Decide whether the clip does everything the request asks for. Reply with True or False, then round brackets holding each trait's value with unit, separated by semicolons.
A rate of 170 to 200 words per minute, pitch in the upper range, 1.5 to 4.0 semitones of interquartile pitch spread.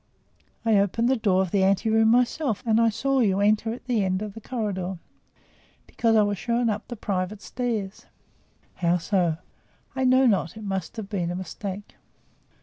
True (185 wpm; 210 Hz; 3.3 semitones)